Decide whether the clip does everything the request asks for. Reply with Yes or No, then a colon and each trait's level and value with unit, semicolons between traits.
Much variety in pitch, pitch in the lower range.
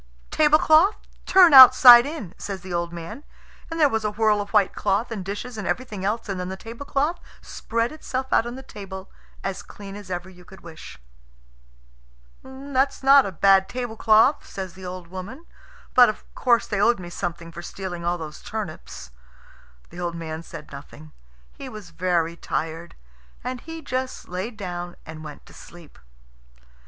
No: wide, 6.1 semitones; high, 200 Hz